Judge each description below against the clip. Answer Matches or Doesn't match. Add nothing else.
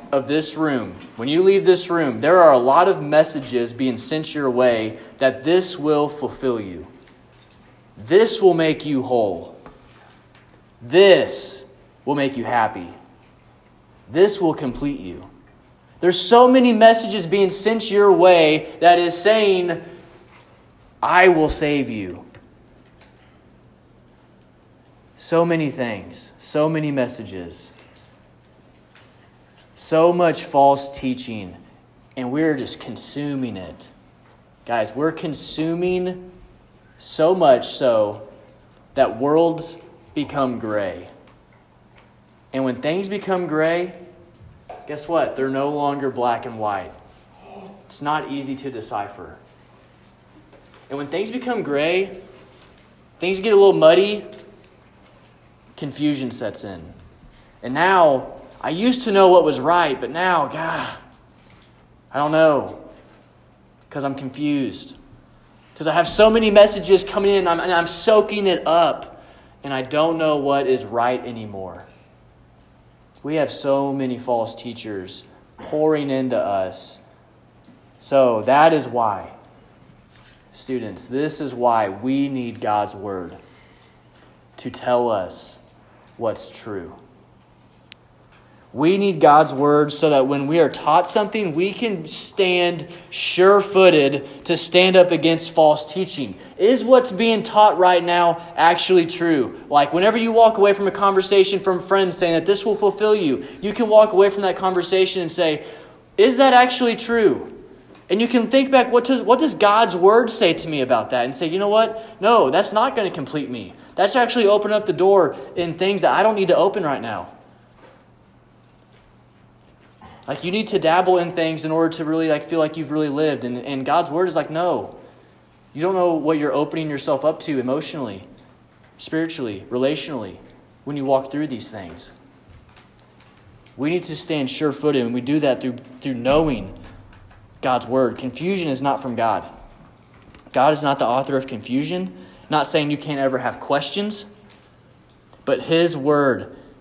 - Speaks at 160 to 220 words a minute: Doesn't match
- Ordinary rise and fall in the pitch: Doesn't match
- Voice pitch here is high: Doesn't match